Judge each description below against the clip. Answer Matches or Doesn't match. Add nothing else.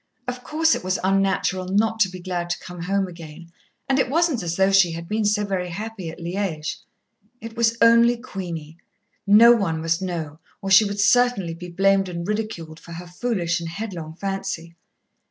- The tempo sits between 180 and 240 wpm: Matches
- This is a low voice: Doesn't match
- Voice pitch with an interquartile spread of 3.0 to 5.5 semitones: Matches